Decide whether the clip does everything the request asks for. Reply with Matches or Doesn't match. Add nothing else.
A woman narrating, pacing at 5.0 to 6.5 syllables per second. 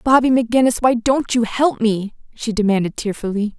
Matches